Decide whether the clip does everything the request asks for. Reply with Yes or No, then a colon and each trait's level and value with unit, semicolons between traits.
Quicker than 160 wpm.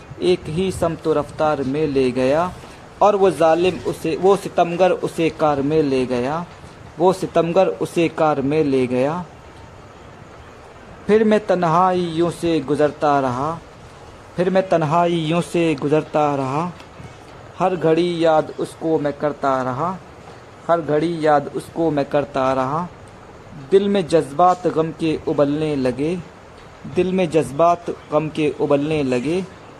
No: average, 135 wpm